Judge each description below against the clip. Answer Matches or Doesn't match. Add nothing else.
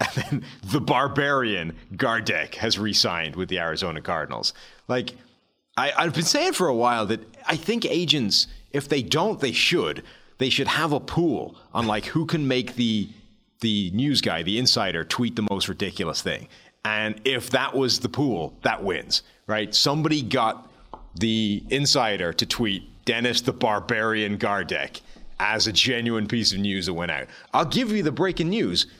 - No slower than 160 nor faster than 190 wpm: Matches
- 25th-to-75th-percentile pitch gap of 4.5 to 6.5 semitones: Matches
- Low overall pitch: Matches